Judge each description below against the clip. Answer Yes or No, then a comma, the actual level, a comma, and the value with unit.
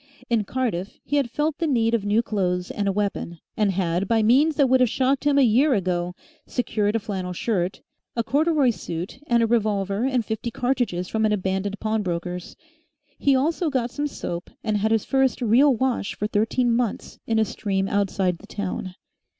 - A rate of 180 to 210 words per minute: Yes, average, 190 wpm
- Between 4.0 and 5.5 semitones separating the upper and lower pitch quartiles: Yes, average, 4.6 semitones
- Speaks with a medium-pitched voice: No, high, 220 Hz